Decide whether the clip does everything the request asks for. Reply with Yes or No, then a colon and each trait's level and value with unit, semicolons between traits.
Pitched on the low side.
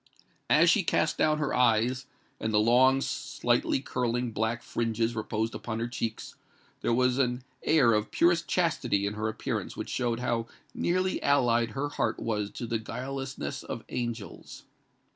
Yes: low, 120 Hz